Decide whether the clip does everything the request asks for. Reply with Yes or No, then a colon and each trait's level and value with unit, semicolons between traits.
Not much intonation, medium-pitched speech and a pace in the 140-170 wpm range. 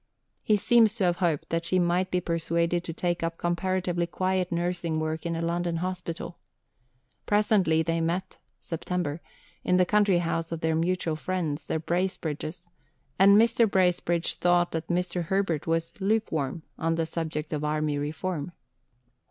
Yes: narrow, 2.1 semitones; medium, 170 Hz; average, 155 wpm